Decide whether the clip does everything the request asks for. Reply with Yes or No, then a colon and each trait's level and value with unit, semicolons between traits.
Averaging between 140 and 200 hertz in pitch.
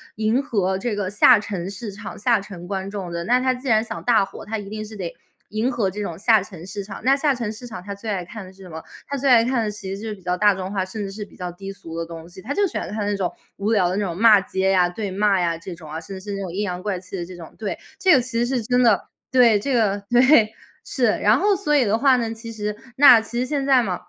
No: high, 210 Hz